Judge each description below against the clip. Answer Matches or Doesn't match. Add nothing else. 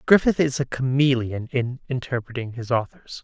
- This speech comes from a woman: Doesn't match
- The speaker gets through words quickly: Doesn't match